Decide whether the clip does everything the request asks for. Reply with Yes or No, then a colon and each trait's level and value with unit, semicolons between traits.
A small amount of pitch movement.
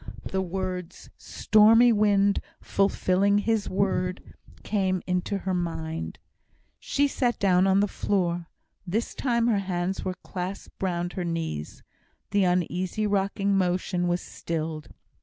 Yes: narrow, 2.3 semitones